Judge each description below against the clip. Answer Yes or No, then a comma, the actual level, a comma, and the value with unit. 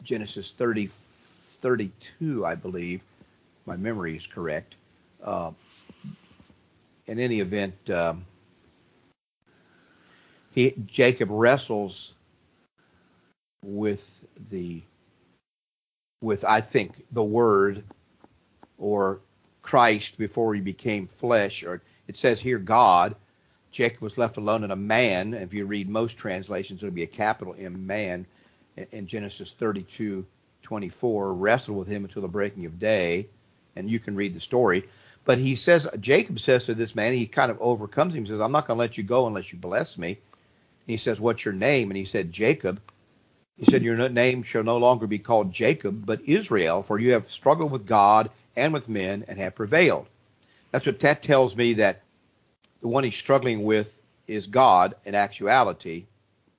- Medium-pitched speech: No, low, 105 Hz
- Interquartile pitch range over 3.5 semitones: No, average, 3.2 semitones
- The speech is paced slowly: No, average, 155 wpm